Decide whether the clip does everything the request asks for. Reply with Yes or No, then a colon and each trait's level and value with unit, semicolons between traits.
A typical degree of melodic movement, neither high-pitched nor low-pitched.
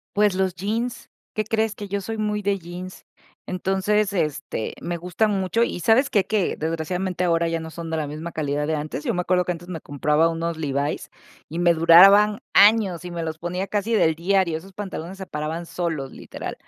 Yes: average, 3.7 semitones; medium, 180 Hz